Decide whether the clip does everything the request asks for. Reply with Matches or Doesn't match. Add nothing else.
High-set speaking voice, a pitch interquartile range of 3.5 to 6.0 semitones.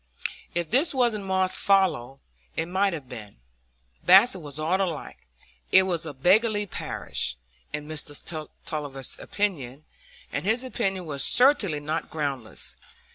Doesn't match